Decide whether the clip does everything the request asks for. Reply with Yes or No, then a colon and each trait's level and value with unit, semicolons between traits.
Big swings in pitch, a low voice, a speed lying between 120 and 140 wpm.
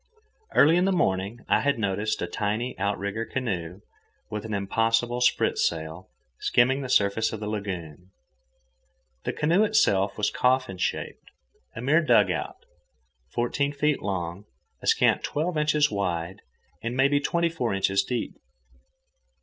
Yes: wide, 6.1 semitones; low, 110 Hz; slow, 135 wpm